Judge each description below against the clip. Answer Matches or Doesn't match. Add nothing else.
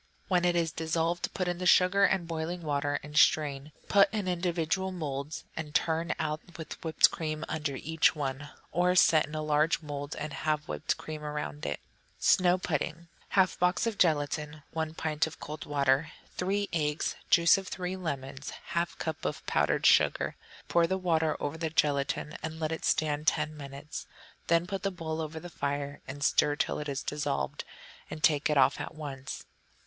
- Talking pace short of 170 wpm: Doesn't match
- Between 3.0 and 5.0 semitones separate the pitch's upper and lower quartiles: Doesn't match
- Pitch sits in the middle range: Matches